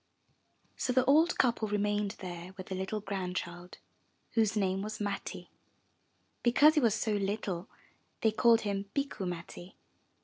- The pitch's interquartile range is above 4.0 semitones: No, average, 3.3 semitones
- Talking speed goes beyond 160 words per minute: No, average, 145 wpm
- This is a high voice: Yes, high, 205 Hz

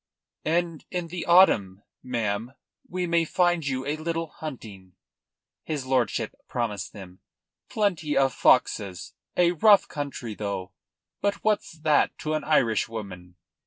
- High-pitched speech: No, medium, 140 Hz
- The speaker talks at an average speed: No, slow, 125 wpm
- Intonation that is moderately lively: No, wide, 7.9 semitones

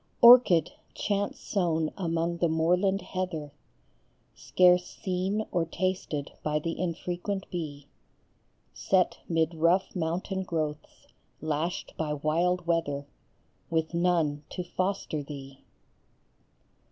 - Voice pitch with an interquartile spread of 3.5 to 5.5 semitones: No, average, 2.7 semitones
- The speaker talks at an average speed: No, slow, 105 wpm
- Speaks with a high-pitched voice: No, medium, 170 Hz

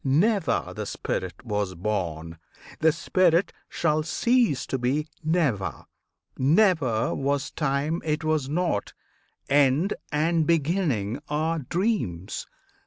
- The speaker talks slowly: Yes, slow, 105 wpm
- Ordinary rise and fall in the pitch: No, wide, 5.8 semitones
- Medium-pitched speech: Yes, medium, 150 Hz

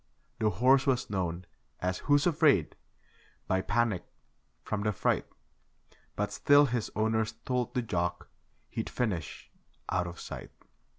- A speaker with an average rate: No, slow, 130 wpm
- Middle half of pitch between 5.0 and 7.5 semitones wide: Yes, wide, 5.4 semitones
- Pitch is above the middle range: No, low, 110 Hz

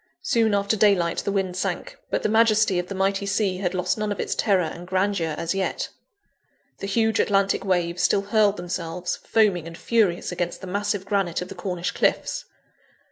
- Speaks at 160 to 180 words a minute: No, average, 190 wpm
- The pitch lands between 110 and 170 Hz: No, high, 195 Hz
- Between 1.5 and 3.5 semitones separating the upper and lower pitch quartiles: Yes, narrow, 2.4 semitones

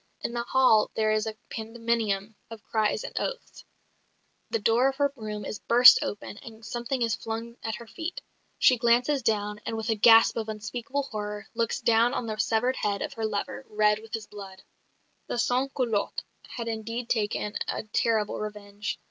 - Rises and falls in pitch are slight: Yes, narrow, 2.1 semitones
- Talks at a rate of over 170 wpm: Yes, average, 180 wpm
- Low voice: No, high, 225 Hz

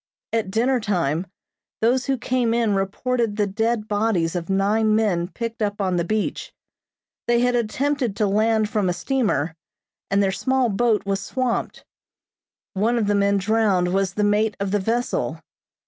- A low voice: No, high, 215 Hz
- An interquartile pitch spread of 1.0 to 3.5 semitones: Yes, average, 3.1 semitones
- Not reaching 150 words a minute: No, average, 165 wpm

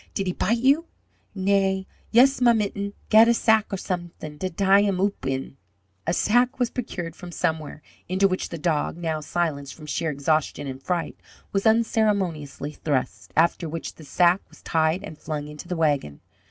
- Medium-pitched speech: Yes, medium, 175 Hz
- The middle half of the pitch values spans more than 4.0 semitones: Yes, average, 4.7 semitones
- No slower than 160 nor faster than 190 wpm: Yes, average, 180 wpm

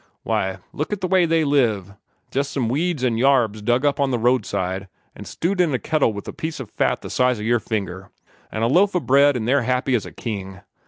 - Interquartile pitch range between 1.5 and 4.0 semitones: No, average, 4.9 semitones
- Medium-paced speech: No, fast, 235 wpm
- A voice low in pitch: Yes, low, 125 Hz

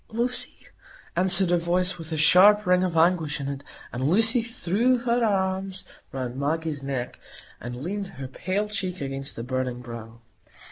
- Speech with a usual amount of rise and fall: No, wide, 6.2 semitones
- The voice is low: No, medium, 175 Hz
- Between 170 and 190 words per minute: No, average, 160 wpm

